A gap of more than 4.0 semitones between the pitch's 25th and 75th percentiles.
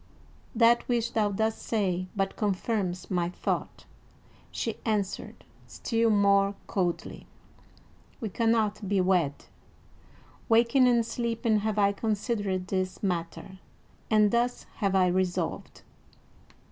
No: average, 3.3 semitones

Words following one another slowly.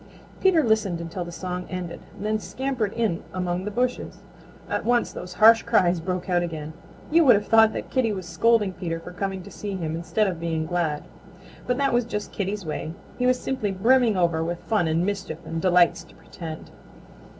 No: average, 195 wpm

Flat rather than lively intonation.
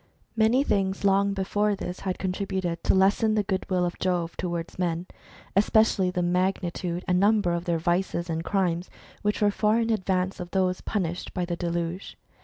Yes: narrow, 2.3 semitones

